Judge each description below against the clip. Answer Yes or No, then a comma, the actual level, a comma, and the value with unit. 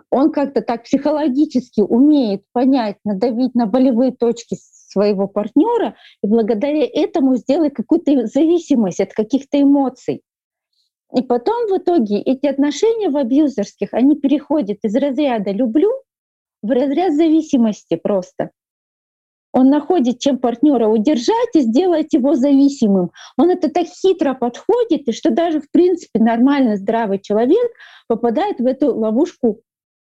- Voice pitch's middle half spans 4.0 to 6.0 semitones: Yes, average, 4.9 semitones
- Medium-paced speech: Yes, average, 125 wpm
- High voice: Yes, very high, 270 Hz